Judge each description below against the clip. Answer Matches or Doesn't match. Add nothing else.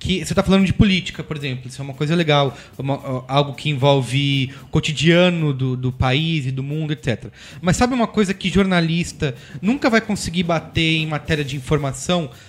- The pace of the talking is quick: Matches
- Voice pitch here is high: Doesn't match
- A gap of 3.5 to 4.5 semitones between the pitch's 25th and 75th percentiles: Matches